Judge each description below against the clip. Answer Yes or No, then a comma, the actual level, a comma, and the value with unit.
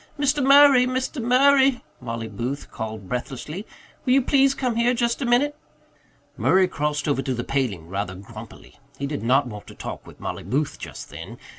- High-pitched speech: No, medium, 150 Hz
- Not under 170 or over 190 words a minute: Yes, average, 180 wpm